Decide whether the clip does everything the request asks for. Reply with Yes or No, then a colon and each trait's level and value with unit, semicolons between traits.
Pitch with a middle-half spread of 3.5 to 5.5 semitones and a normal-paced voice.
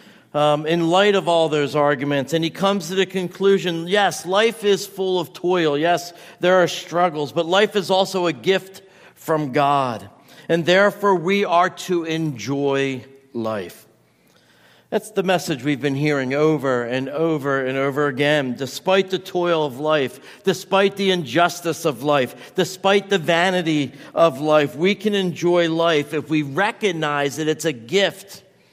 Yes: average, 4.3 semitones; average, 160 wpm